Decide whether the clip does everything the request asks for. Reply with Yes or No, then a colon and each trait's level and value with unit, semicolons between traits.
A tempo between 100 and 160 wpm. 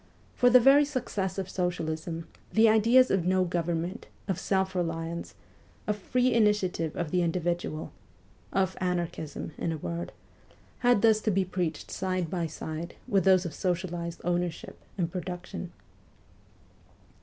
Yes: average, 140 wpm